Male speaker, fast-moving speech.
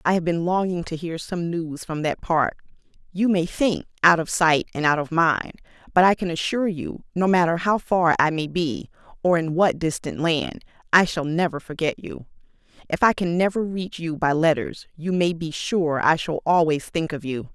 No: female; fast, 210 wpm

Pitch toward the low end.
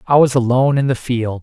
Yes: low, 130 Hz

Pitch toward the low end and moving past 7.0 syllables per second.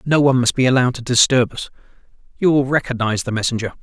Yes: low, 125 Hz; 7.4 syllables/s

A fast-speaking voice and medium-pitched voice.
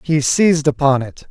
No: average, 185 wpm; medium, 145 Hz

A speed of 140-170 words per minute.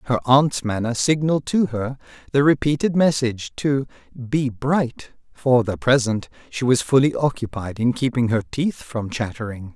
Yes: average, 155 wpm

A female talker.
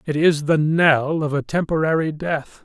No: male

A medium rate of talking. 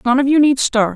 No: fast, 315 wpm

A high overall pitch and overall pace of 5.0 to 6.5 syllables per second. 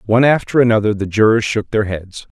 No: low, 110 Hz; 6.0 syllables/s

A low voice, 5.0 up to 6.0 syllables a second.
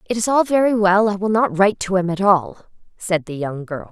No: high, 195 Hz; 5.5 syllables/s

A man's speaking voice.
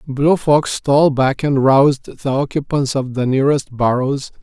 Yes: male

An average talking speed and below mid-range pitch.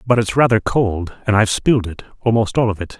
No: fast, 220 wpm; low, 110 Hz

